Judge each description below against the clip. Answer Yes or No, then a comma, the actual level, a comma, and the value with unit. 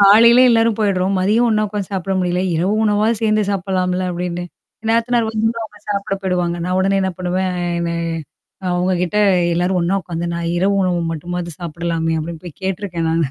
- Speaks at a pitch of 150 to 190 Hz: Yes, medium, 185 Hz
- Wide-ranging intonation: No, average, 3.1 semitones